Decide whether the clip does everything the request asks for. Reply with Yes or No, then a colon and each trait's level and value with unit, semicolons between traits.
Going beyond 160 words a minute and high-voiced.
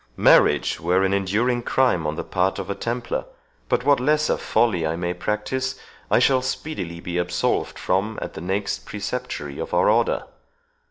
No: average, 170 wpm; low, 100 Hz